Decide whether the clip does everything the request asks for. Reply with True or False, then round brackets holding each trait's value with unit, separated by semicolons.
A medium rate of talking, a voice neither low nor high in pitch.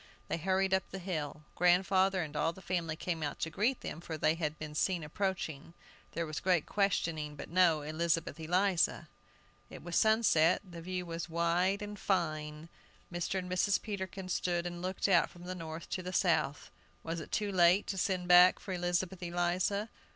True (185 wpm; 175 Hz)